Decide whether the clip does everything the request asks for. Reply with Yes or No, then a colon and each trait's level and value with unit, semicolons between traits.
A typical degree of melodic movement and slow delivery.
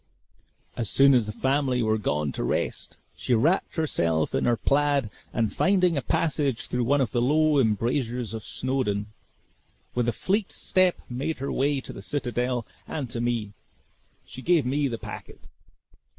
No: average, 4.1 semitones; average, 165 wpm